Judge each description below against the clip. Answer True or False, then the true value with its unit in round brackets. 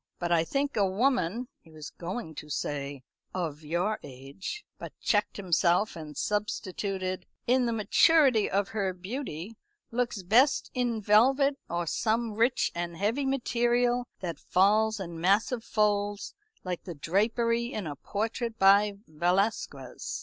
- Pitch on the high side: True (205 Hz)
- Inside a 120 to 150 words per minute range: True (140 wpm)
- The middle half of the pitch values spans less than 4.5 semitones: False (5.2 semitones)